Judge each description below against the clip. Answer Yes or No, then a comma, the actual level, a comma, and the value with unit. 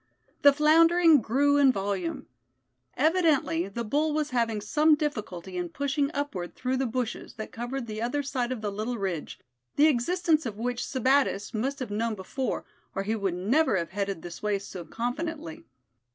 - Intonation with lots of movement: Yes, wide, 5.9 semitones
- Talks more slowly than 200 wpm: Yes, average, 170 wpm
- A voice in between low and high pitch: No, high, 245 Hz